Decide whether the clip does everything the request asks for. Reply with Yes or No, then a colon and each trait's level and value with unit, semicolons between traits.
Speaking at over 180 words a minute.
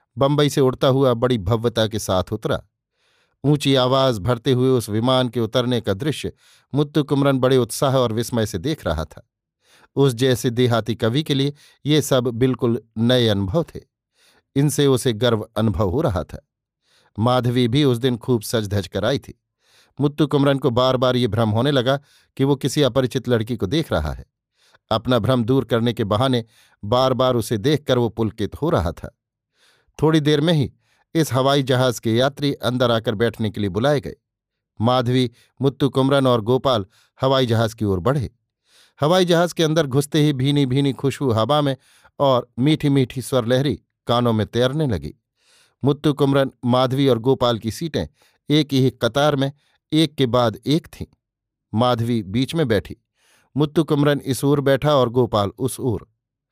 No: average, 175 wpm